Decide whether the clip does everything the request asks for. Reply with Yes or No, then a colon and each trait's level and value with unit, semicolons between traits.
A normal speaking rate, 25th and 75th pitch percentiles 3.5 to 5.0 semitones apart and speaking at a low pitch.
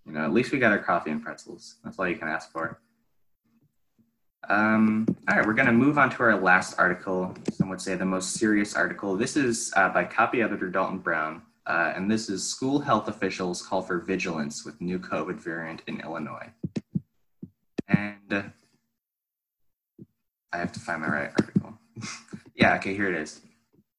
No: average, 185 wpm; average, 3.0 semitones; very low, 95 Hz